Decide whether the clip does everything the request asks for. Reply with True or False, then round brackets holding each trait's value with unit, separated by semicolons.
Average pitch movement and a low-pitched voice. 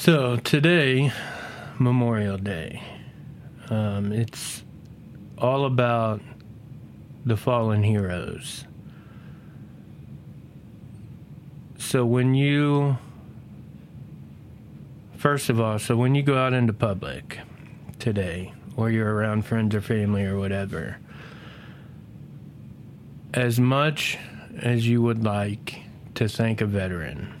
True (4.0 semitones; 120 Hz)